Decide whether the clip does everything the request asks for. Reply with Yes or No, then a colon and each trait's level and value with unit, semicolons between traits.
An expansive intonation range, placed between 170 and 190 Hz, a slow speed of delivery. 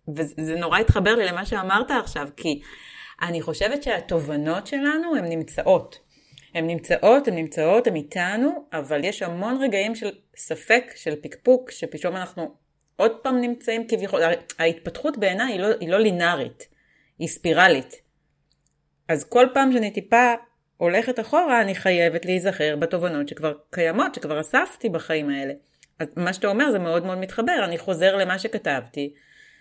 No: wide, 6.1 semitones; medium, 185 Hz; average, 145 wpm